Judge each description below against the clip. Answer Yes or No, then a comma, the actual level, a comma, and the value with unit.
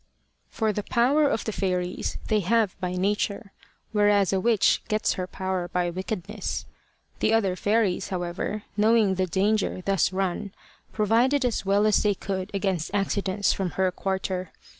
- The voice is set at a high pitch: Yes, high, 200 Hz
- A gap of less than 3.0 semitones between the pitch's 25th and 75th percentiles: Yes, narrow, 2.4 semitones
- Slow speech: No, average, 155 wpm